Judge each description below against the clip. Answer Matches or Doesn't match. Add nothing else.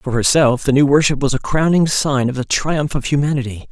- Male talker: Matches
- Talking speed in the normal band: Doesn't match